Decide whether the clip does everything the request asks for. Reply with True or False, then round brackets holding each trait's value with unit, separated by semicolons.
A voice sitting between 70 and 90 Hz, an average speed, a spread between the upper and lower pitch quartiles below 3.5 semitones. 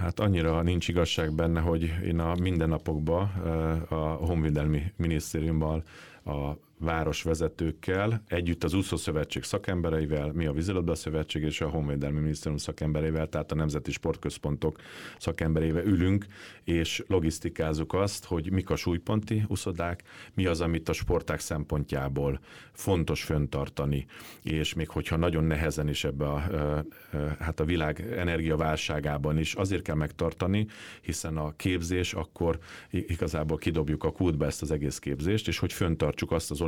True (80 Hz; 140 wpm; 2.4 semitones)